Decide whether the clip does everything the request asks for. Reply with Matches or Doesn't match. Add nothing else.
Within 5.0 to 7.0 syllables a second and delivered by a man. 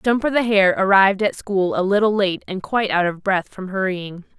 Doesn't match